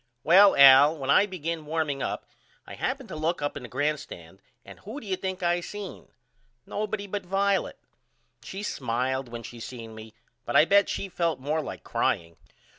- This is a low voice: No, medium, 155 Hz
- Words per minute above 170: Yes, average, 190 wpm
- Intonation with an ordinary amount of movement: No, wide, 6.4 semitones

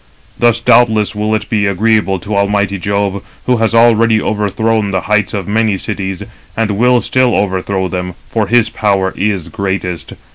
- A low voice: Yes, low, 105 Hz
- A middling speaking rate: Yes, average, 160 wpm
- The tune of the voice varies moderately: No, narrow, 2.3 semitones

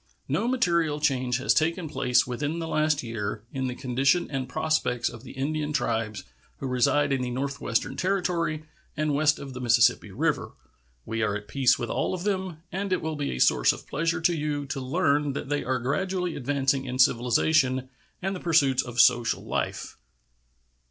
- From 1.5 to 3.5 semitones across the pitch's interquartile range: No, average, 4.1 semitones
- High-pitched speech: No, medium, 140 Hz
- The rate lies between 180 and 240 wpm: Yes, average, 185 wpm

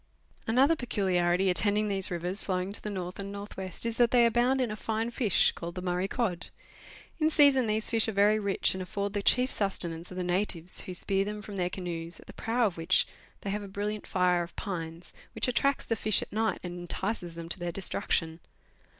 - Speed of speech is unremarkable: No, fast, 220 wpm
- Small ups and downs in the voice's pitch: No, average, 3.5 semitones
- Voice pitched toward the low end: No, high, 200 Hz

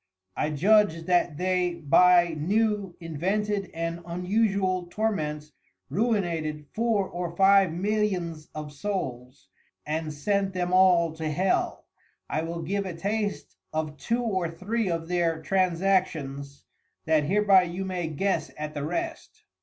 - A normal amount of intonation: Yes, average, 3.7 semitones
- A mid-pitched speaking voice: Yes, medium, 175 Hz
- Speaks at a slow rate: Yes, slow, 130 wpm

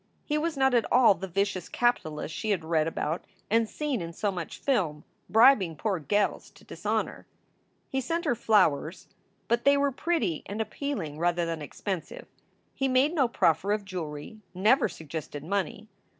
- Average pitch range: No, wide, 7.5 semitones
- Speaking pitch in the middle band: No, high, 200 Hz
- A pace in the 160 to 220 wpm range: Yes, average, 165 wpm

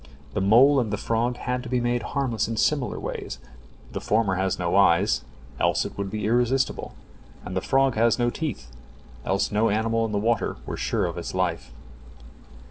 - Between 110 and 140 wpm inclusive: No, average, 185 wpm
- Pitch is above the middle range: No, low, 115 Hz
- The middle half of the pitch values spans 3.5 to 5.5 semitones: Yes, average, 3.8 semitones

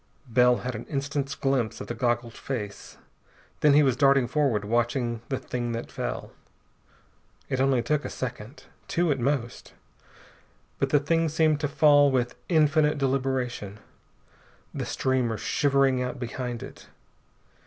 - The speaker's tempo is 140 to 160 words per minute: Yes, average, 145 wpm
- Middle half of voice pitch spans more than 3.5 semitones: No, average, 3.1 semitones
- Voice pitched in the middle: No, low, 130 Hz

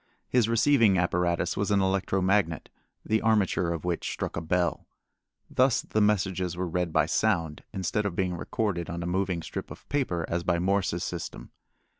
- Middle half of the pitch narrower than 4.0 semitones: Yes, average, 3.0 semitones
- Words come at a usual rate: Yes, average, 175 wpm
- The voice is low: Yes, very low, 90 Hz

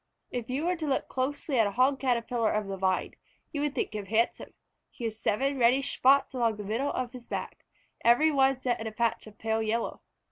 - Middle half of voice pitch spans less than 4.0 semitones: Yes, average, 3.4 semitones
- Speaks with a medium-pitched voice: No, high, 240 Hz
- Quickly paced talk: Yes, fast, 220 wpm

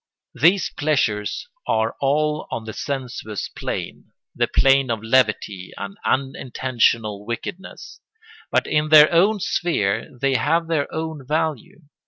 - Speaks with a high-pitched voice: No, low, 135 Hz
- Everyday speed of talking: No, slow, 125 wpm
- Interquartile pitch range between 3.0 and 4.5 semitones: No, wide, 5.6 semitones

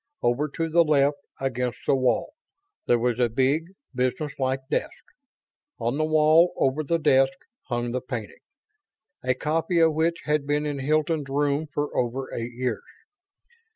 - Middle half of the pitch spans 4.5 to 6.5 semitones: No, average, 3.5 semitones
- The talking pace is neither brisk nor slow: Yes, average, 155 wpm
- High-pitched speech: No, medium, 140 Hz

